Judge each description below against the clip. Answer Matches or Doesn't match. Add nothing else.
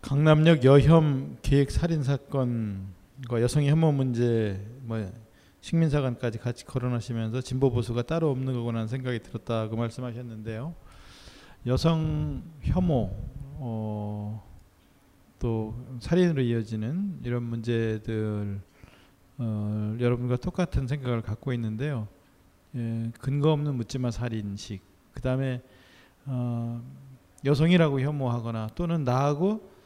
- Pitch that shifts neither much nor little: Matches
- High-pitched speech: Doesn't match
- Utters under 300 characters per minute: Matches